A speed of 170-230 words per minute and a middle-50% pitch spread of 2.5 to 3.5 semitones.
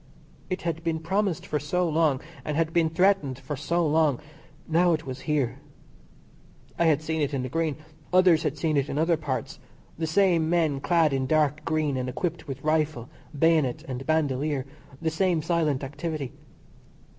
Yes: average, 175 wpm; average, 2.9 semitones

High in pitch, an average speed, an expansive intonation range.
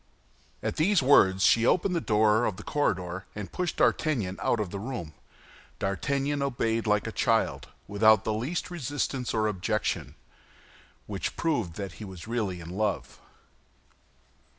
No: low, 110 Hz; average, 150 wpm; wide, 6.0 semitones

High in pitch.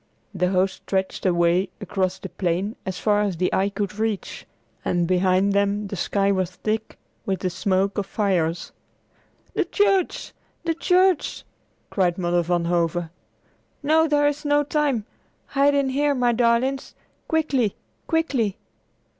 Yes: high, 200 Hz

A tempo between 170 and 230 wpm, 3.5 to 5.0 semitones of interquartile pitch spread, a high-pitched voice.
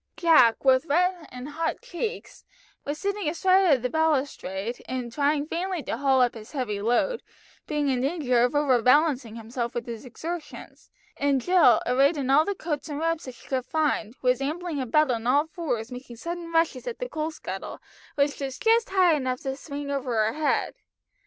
Yes: average, 190 wpm; average, 4.7 semitones; very high, 285 Hz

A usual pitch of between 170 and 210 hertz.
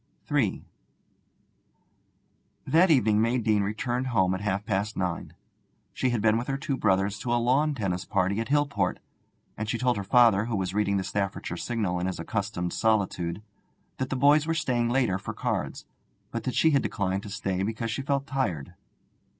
No: low, 110 Hz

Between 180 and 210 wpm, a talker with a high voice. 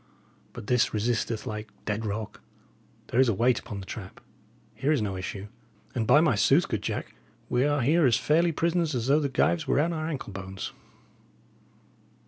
No: average, 185 wpm; low, 125 Hz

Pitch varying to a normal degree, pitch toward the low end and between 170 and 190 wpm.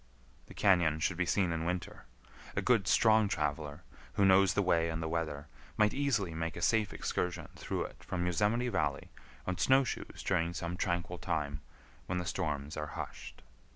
Yes: average, 3.5 semitones; very low, 90 Hz; average, 180 wpm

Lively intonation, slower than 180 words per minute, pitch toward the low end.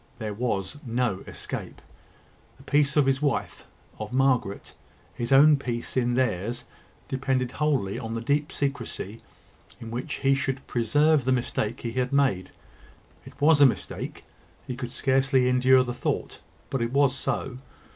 No: average, 2.7 semitones; average, 155 wpm; low, 130 Hz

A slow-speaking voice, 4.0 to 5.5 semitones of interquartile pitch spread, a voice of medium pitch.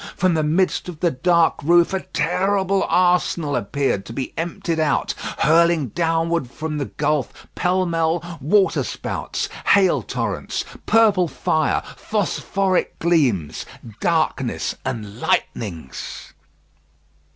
No: slow, 110 wpm; average, 3.6 semitones; medium, 165 Hz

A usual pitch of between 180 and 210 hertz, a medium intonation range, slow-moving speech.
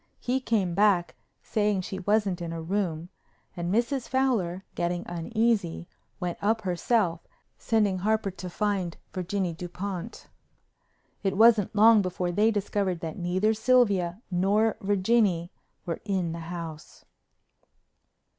Yes: high, 190 Hz; average, 3.6 semitones; slow, 125 wpm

